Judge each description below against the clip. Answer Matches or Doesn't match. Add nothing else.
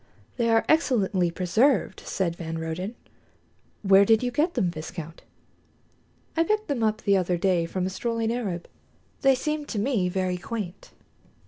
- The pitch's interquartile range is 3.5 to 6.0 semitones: Matches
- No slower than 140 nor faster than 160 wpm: Matches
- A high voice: Matches